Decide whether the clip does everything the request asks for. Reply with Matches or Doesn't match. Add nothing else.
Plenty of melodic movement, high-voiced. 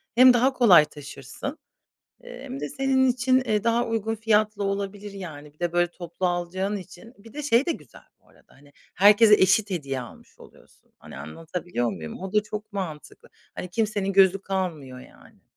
Doesn't match